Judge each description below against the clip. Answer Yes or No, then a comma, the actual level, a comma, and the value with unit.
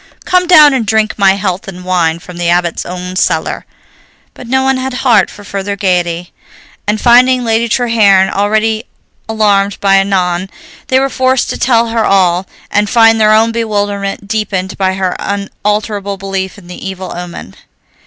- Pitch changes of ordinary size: Yes, average, 3.1 semitones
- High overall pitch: Yes, high, 200 Hz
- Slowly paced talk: No, average, 165 wpm